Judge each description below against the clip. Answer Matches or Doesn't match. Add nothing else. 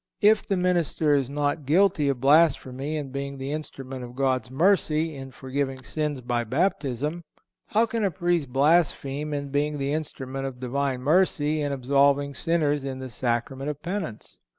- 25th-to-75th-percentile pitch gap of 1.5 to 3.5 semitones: Matches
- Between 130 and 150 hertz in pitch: Matches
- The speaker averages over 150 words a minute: Matches